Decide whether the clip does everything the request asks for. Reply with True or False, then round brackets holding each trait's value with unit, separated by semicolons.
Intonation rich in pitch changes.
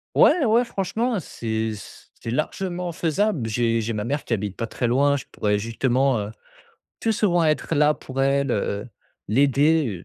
True (6.6 semitones)